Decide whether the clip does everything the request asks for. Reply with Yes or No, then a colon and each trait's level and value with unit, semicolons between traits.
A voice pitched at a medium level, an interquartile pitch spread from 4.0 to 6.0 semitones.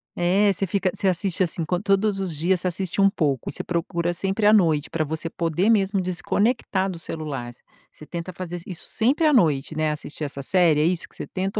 No: medium, 180 Hz; average, 3.3 semitones